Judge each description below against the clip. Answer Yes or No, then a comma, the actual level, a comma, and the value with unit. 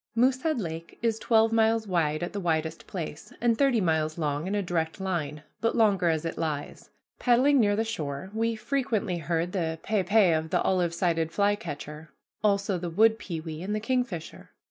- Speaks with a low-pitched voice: No, medium, 185 Hz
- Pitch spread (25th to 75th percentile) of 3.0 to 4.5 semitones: No, wide, 5.4 semitones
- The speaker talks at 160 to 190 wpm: Yes, average, 185 wpm